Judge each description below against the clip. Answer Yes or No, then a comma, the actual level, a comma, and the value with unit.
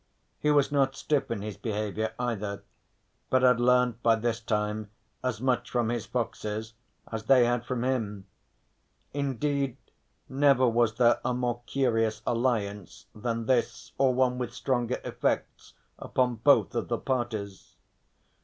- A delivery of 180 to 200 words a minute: No, average, 145 wpm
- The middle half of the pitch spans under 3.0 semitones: Yes, narrow, 2.5 semitones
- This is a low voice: Yes, low, 120 Hz